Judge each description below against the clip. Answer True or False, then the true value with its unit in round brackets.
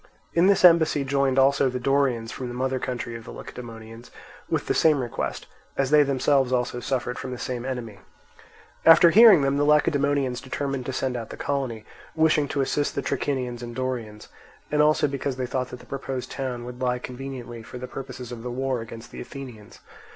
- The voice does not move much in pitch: True (2.3 semitones)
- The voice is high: False (130 Hz)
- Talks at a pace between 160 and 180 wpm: False (195 wpm)